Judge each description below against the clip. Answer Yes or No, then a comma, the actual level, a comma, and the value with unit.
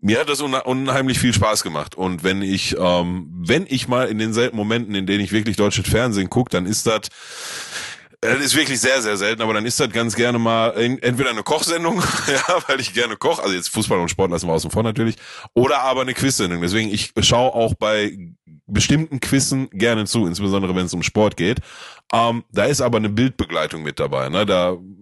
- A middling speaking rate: No, fast, 205 wpm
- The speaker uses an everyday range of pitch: Yes, average, 4.2 semitones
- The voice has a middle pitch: No, low, 110 Hz